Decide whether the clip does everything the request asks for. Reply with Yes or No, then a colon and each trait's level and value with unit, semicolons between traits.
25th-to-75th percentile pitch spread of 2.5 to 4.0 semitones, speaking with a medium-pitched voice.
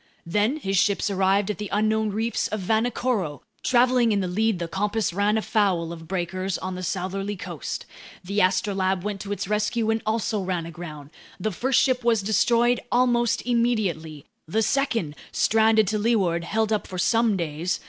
No: average, 3.4 semitones; high, 205 Hz